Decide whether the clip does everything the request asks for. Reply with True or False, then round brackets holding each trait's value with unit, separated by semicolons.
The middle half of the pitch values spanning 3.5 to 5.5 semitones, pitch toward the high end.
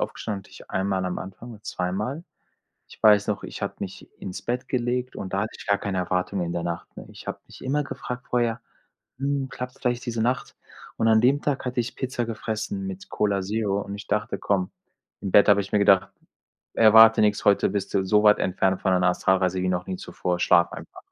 False (4.4 semitones; 105 Hz)